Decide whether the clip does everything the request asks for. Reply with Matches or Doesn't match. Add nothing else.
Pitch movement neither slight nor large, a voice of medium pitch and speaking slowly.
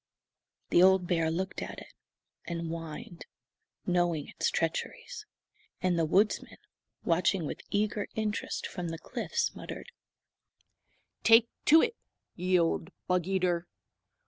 Matches